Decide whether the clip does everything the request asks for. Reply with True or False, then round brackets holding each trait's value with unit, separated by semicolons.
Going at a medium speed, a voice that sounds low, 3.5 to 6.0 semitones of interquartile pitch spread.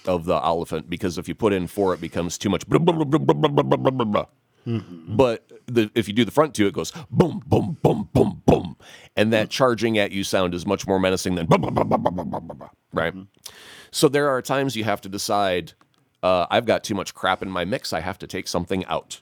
True (195 wpm; 100 Hz; 4.5 semitones)